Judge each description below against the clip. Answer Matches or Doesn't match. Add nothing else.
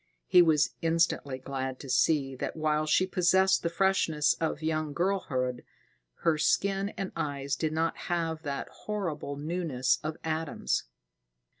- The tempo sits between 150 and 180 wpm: Doesn't match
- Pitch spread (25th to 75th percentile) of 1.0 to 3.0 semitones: Doesn't match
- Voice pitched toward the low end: Doesn't match